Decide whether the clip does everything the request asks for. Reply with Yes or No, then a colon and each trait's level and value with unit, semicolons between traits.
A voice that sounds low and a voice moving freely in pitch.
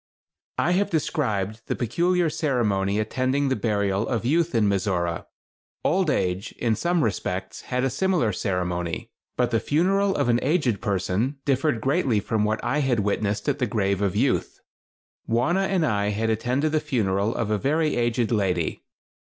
Yes: low, 120 Hz; wide, 6.6 semitones